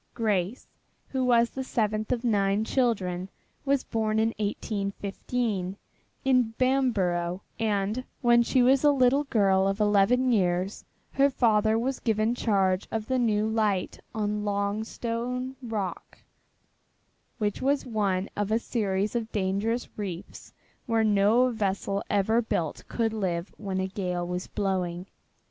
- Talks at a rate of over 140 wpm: No, slow, 135 wpm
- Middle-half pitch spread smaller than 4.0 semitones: Yes, average, 3.4 semitones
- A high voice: Yes, high, 215 Hz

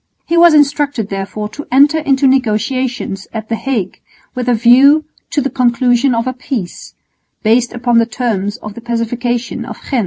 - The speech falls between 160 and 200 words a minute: Yes, average, 175 wpm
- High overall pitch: Yes, high, 245 Hz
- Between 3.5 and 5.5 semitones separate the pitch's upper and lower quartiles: No, average, 3.0 semitones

